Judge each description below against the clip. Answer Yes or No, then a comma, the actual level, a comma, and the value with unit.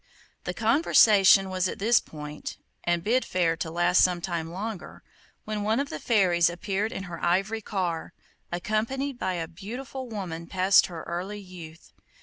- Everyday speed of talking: Yes, average, 160 wpm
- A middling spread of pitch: Yes, average, 3.8 semitones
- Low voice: No, medium, 185 Hz